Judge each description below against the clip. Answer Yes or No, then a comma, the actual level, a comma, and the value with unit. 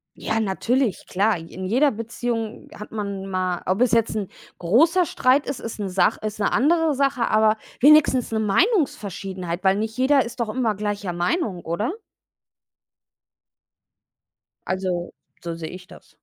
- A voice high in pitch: Yes, high, 215 Hz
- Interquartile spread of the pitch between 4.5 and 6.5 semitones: Yes, average, 5.1 semitones